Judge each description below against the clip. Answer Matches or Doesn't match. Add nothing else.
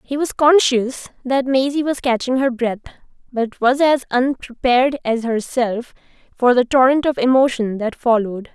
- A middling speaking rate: Matches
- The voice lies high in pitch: Matches